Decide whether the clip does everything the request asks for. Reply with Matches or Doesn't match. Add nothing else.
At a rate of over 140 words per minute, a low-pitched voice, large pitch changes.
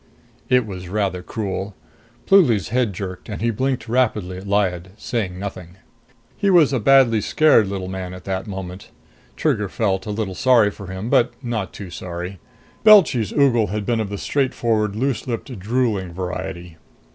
Doesn't match